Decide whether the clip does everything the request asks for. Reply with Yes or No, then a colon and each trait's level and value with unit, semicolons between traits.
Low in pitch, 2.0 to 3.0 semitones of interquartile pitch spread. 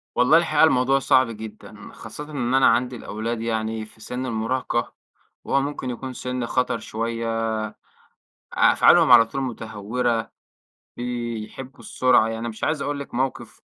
Yes: low, 120 Hz; narrow, 2.5 semitones